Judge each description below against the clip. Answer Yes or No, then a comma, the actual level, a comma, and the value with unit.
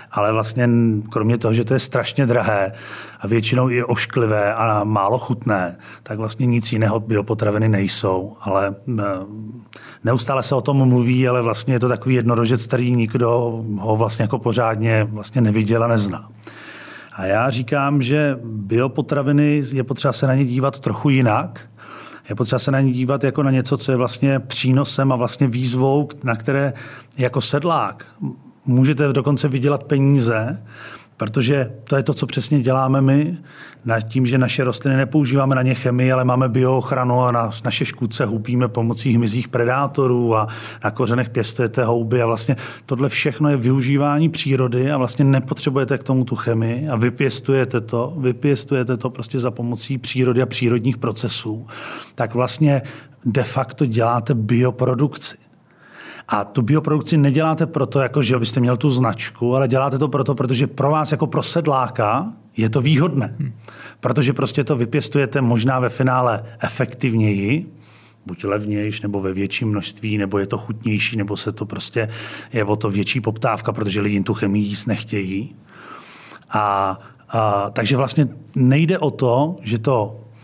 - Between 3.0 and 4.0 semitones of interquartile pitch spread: Yes, average, 3.4 semitones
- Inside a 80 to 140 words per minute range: No, average, 160 wpm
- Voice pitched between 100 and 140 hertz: Yes, low, 125 Hz